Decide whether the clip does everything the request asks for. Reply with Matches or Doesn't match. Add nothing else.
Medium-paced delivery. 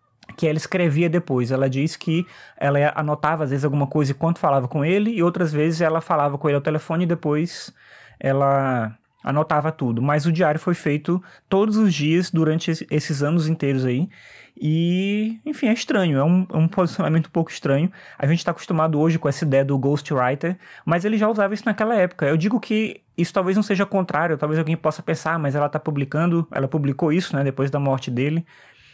Doesn't match